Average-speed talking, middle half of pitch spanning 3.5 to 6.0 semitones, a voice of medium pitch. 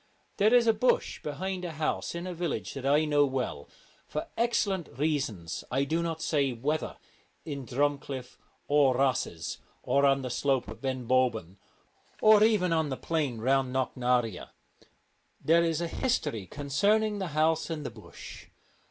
Yes: average, 160 wpm; average, 4.5 semitones; medium, 145 Hz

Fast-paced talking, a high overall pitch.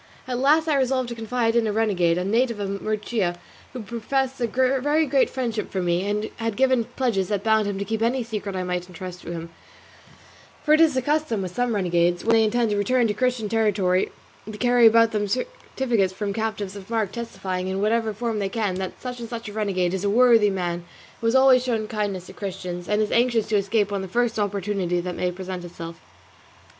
Yes: fast, 220 wpm; high, 215 Hz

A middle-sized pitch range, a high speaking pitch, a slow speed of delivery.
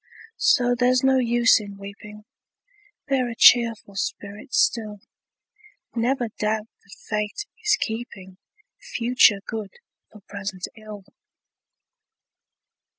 Yes: average, 3.1 semitones; high, 220 Hz; slow, 100 wpm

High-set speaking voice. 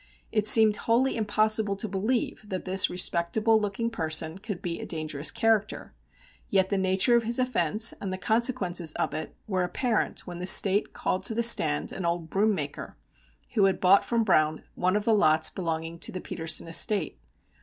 Yes: high, 195 Hz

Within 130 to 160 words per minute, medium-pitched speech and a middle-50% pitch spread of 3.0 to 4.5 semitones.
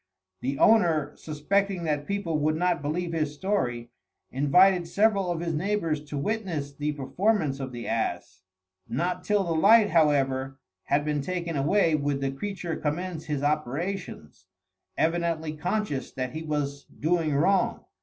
Yes: average, 145 wpm; medium, 155 Hz; average, 4.1 semitones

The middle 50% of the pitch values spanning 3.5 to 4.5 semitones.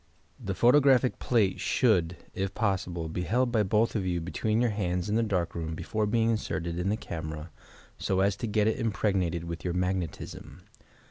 Yes: average, 4.1 semitones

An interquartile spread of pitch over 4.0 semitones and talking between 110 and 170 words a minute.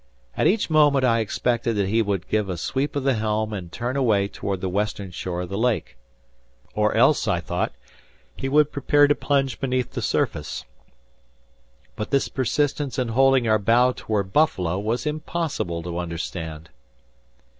Yes: wide, 5.5 semitones; average, 165 wpm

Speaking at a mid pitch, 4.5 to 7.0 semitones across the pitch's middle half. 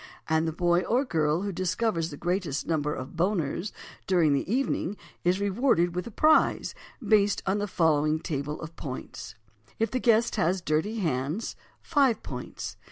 Yes: medium, 175 Hz; average, 4.9 semitones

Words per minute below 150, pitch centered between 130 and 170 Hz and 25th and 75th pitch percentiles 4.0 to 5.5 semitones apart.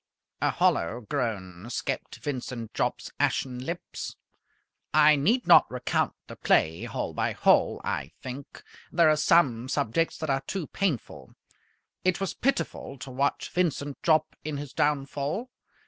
Yes: average, 140 wpm; medium, 140 Hz; average, 4.7 semitones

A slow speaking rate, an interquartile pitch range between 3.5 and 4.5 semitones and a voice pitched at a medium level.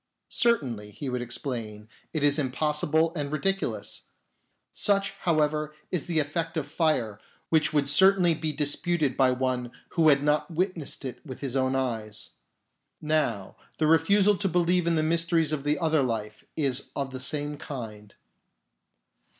No: average, 160 wpm; average, 4.1 semitones; medium, 150 Hz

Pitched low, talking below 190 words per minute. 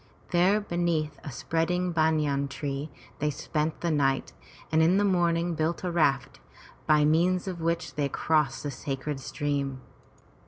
No: medium, 155 Hz; average, 150 wpm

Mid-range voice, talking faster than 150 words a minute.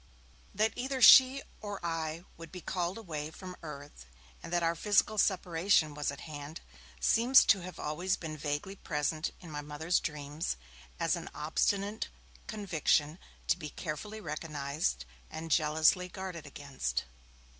No: medium, 165 Hz; average, 145 wpm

